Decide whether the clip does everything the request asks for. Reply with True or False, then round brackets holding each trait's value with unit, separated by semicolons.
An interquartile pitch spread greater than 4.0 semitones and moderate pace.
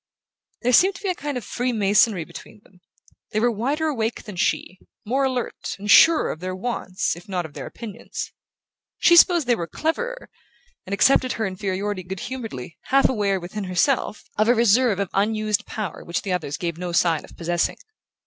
True (5.4 semitones; 185 wpm)